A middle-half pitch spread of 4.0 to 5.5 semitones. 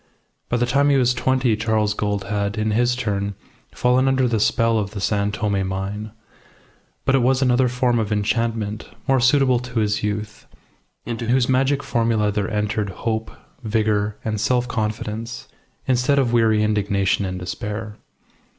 No: average, 3.0 semitones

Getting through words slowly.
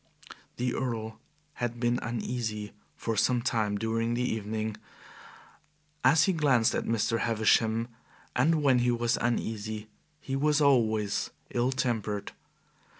Yes: slow, 125 wpm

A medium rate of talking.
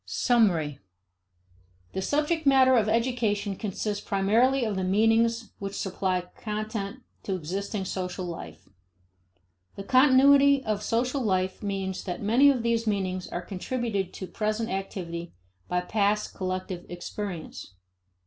No: slow, 125 wpm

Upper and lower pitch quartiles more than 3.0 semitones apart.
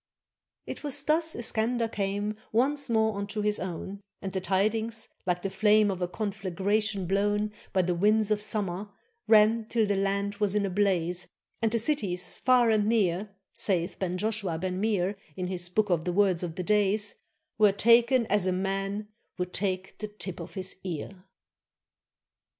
No: narrow, 2.5 semitones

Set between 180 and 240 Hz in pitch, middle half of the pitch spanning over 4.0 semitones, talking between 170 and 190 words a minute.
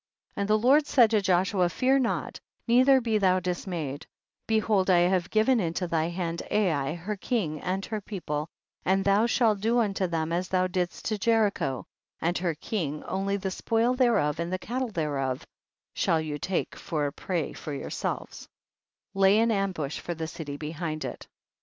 Yes: medium, 185 Hz; average, 4.8 semitones; average, 180 wpm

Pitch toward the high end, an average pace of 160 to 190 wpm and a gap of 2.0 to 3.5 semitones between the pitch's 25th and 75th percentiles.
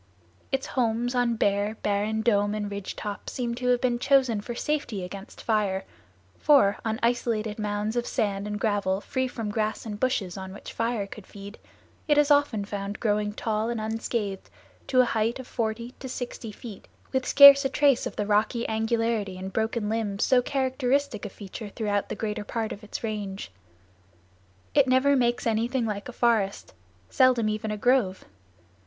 Yes: high, 220 Hz; average, 175 wpm; average, 3.0 semitones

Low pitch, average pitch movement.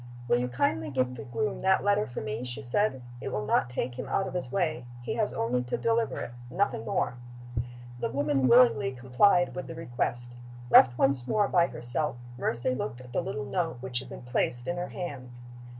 No: low, 130 Hz; wide, 6.1 semitones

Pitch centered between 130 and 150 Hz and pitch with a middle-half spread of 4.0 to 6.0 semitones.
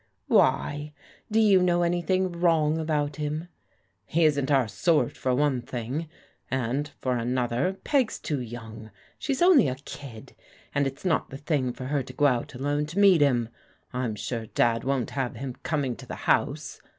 Yes: medium, 140 Hz; average, 4.6 semitones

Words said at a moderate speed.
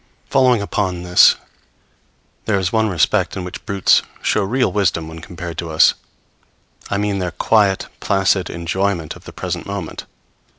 Yes: average, 155 wpm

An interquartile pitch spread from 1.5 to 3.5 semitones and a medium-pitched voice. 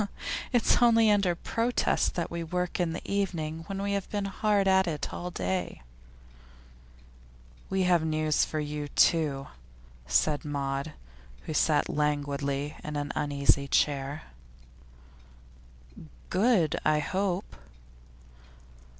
No: average, 4.6 semitones; medium, 160 Hz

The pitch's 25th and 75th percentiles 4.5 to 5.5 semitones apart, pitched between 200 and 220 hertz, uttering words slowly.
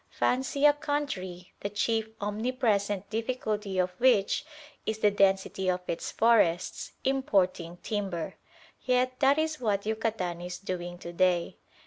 Yes: average, 5.2 semitones; high, 205 Hz; slow, 130 wpm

